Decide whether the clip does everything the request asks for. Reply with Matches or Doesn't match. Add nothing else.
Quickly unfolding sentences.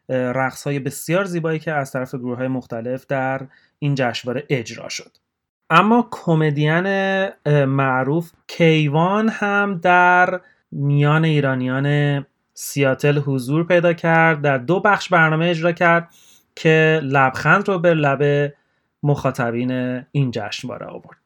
Doesn't match